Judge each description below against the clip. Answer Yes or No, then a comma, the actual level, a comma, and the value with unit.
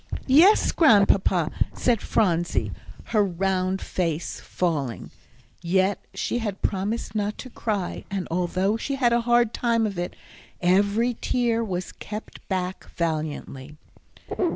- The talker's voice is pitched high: Yes, high, 195 Hz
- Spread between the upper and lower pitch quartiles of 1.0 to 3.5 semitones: No, average, 4.4 semitones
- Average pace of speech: No, slow, 125 wpm